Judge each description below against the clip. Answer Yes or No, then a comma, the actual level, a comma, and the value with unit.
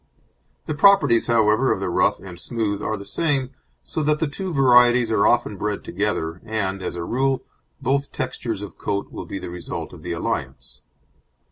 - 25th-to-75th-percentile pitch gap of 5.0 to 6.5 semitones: Yes, wide, 5.5 semitones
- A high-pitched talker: No, low, 110 Hz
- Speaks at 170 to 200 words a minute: Yes, average, 180 wpm